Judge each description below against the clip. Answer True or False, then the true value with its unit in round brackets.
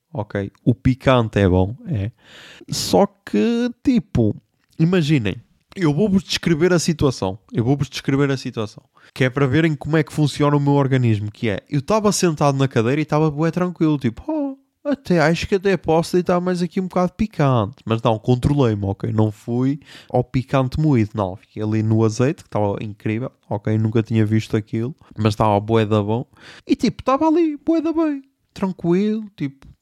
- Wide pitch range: True (8.0 semitones)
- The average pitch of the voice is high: False (140 Hz)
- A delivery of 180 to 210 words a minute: True (185 wpm)